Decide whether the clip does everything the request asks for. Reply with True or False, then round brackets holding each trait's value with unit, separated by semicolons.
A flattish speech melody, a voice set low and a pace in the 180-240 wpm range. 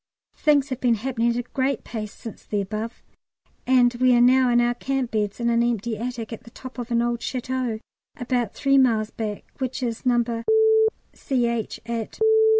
False (2.0 semitones; 240 Hz; 185 wpm)